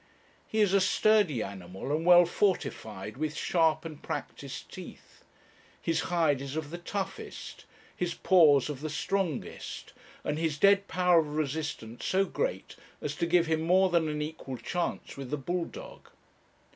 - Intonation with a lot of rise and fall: No, average, 3.6 semitones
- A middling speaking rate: Yes, average, 160 wpm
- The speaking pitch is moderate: Yes, medium, 160 Hz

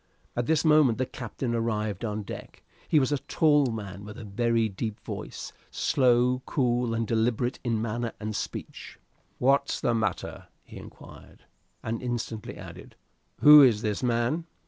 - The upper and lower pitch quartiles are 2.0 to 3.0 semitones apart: Yes, average, 2.7 semitones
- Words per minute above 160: No, average, 155 wpm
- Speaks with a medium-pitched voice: No, low, 120 Hz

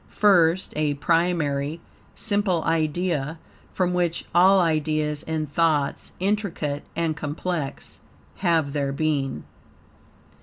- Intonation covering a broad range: No, average, 3.0 semitones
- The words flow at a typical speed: No, slow, 100 wpm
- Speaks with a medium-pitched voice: Yes, medium, 160 Hz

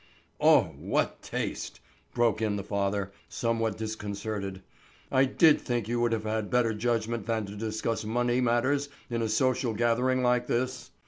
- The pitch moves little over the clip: Yes, narrow, 2.2 semitones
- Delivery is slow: No, average, 150 wpm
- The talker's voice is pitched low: Yes, low, 115 Hz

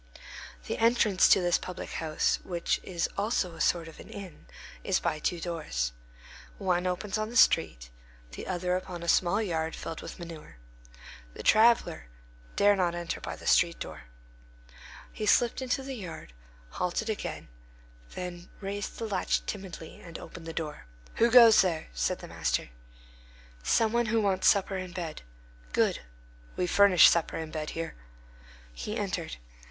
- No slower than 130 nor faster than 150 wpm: No, average, 160 wpm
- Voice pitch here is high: No, medium, 180 Hz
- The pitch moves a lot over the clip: No, average, 3.8 semitones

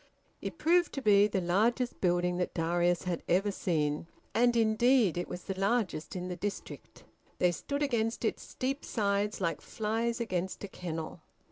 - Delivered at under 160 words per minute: No, average, 165 wpm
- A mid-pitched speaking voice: No, high, 200 Hz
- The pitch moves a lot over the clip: No, average, 4.7 semitones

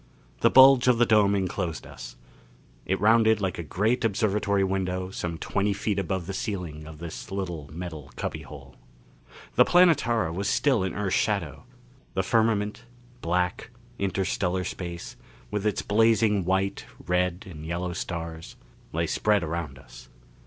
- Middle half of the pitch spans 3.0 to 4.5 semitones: Yes, average, 3.6 semitones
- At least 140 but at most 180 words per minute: Yes, average, 145 wpm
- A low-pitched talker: Yes, very low, 95 Hz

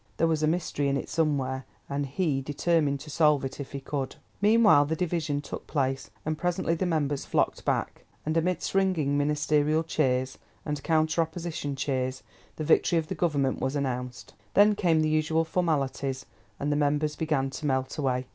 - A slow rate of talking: No, average, 180 wpm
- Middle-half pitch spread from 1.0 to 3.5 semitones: Yes, average, 2.8 semitones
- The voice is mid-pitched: Yes, medium, 150 Hz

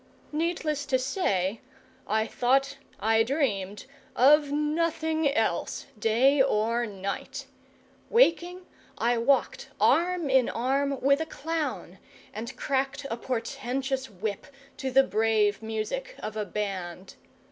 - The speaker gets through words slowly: Yes, slow, 115 wpm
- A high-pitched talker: Yes, very high, 265 Hz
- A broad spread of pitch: No, average, 4.8 semitones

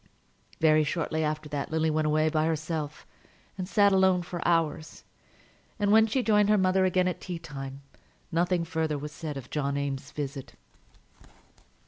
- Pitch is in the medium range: Yes, medium, 160 Hz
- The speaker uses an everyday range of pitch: Yes, average, 3.5 semitones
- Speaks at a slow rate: No, average, 160 wpm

